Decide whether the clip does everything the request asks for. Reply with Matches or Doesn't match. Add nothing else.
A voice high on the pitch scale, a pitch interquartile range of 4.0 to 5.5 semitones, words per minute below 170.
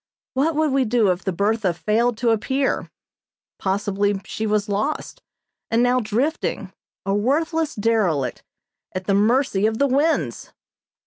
Matches